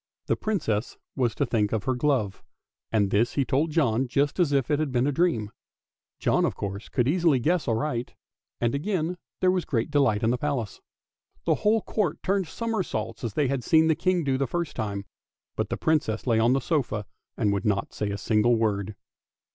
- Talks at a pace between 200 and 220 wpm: Yes, fast, 205 wpm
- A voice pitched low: Yes, low, 130 Hz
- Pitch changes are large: Yes, wide, 6.2 semitones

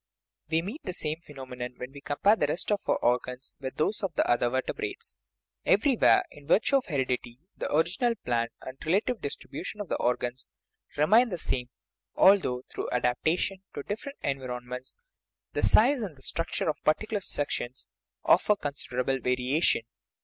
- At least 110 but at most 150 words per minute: No, average, 165 wpm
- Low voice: No, medium, 145 Hz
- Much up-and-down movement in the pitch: Yes, wide, 8.1 semitones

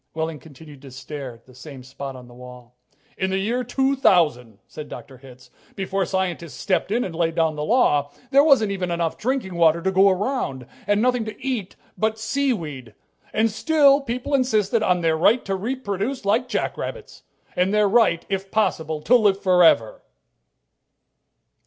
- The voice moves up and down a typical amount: No, wide, 6.9 semitones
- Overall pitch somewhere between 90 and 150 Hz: No, high, 190 Hz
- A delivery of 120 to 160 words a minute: No, average, 170 wpm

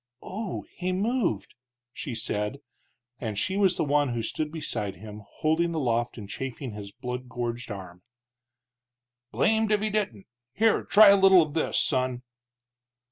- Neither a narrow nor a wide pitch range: No, wide, 8.7 semitones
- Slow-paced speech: No, average, 150 wpm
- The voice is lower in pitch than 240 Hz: Yes, low, 135 Hz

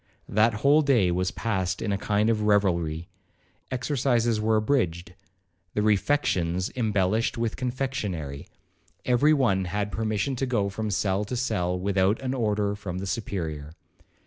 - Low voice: Yes, low, 105 Hz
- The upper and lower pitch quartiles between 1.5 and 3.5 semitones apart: No, average, 4.0 semitones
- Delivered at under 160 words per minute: Yes, slow, 135 wpm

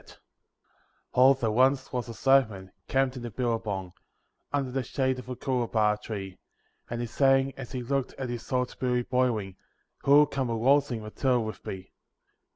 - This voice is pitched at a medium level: No, low, 125 Hz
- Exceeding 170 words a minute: No, average, 165 wpm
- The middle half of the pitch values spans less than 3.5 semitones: Yes, average, 3.1 semitones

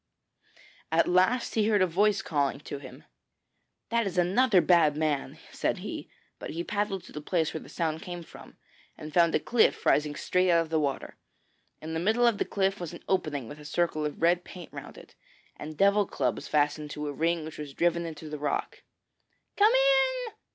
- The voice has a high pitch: No, medium, 170 Hz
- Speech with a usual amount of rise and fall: Yes, average, 4.4 semitones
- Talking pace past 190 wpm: Yes, average, 200 wpm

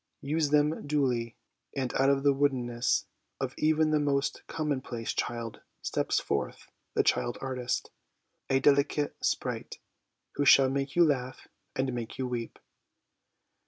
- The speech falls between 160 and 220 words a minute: No, slow, 135 wpm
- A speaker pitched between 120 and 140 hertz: Yes, low, 135 Hz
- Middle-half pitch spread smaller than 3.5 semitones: Yes, average, 2.7 semitones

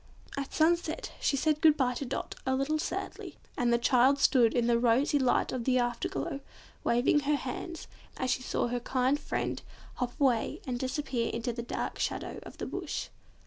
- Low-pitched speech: No, very high, 255 Hz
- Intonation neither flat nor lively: Yes, average, 3.0 semitones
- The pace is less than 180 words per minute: No, average, 195 wpm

